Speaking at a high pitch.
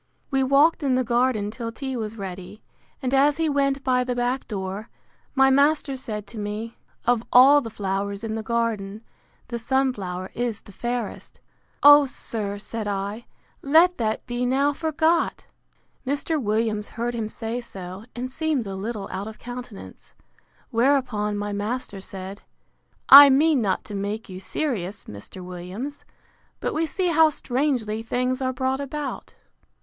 Yes: high, 240 Hz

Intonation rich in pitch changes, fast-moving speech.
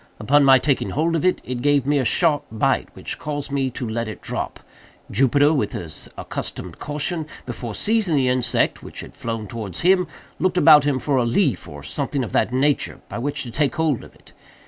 No: average, 4.0 semitones; fast, 210 wpm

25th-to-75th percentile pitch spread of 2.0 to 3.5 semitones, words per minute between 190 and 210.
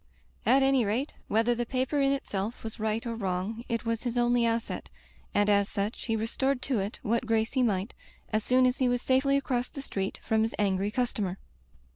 Yes: average, 3.1 semitones; fast, 205 wpm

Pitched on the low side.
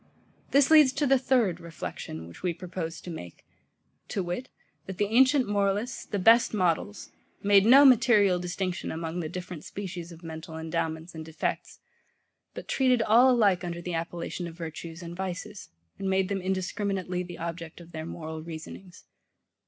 No: medium, 180 Hz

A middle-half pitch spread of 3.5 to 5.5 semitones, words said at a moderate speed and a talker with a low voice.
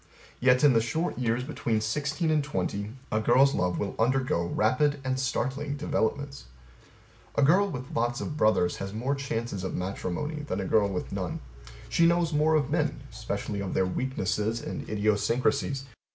Yes: average, 5.1 semitones; average, 165 wpm; low, 125 Hz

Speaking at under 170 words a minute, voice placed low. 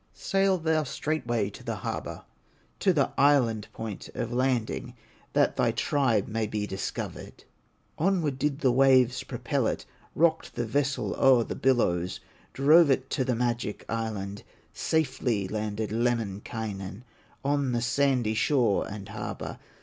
Yes: slow, 135 wpm; low, 120 Hz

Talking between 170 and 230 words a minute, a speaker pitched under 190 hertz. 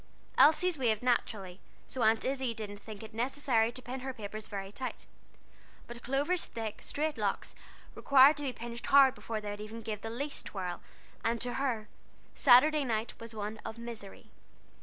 No: average, 175 wpm; high, 235 Hz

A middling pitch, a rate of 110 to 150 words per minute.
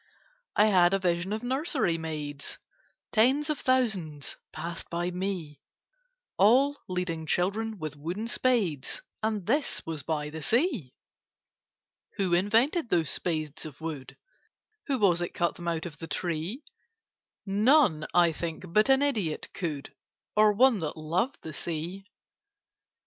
Yes: medium, 180 Hz; average, 140 wpm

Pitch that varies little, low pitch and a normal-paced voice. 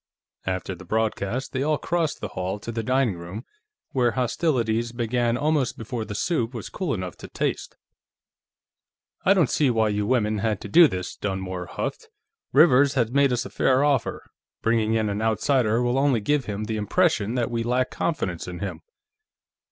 No: average, 4.3 semitones; low, 115 Hz; average, 180 wpm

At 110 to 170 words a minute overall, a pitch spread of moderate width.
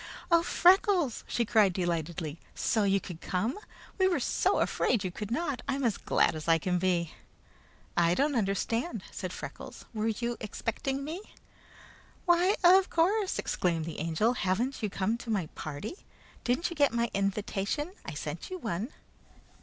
No: average, 160 wpm; wide, 7.9 semitones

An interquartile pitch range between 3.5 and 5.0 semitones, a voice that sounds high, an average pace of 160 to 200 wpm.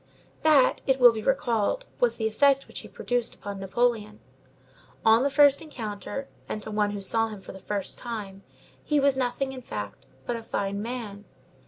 Yes: average, 4.4 semitones; high, 230 Hz; average, 185 wpm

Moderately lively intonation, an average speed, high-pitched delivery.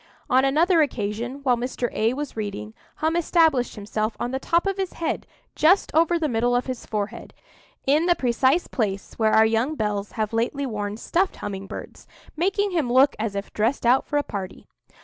No: wide, 6.2 semitones; average, 190 wpm; very high, 250 Hz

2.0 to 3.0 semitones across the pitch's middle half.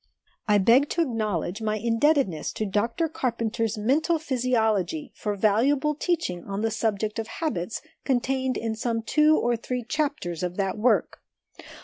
No: average, 4.5 semitones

